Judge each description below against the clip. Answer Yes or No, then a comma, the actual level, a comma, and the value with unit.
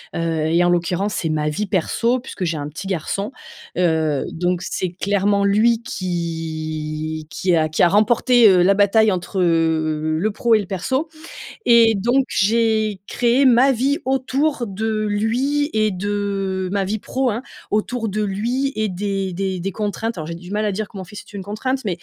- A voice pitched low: No, high, 200 Hz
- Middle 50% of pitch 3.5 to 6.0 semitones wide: Yes, average, 4.2 semitones